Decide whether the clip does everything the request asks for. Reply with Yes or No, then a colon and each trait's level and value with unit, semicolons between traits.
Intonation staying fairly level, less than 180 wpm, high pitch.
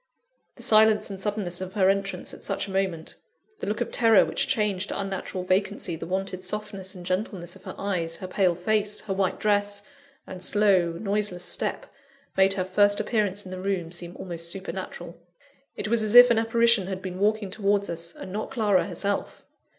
No: narrow, 2.2 semitones; average, 190 wpm; high, 195 Hz